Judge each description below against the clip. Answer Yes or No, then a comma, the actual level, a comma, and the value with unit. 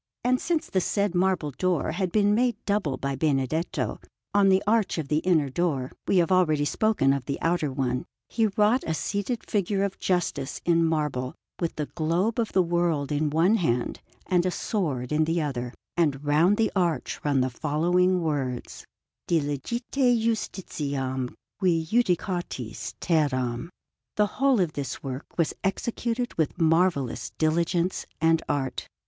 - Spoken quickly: No, average, 155 wpm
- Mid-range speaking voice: Yes, medium, 165 Hz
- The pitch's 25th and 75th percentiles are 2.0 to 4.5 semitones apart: No, average, 5.2 semitones